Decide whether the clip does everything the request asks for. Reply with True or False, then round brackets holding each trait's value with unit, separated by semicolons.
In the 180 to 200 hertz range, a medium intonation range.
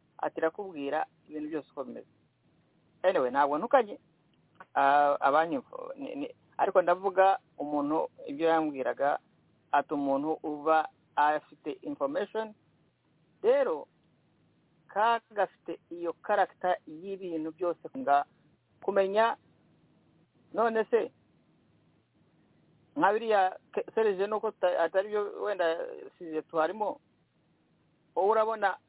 False (190 Hz; 5.8 semitones)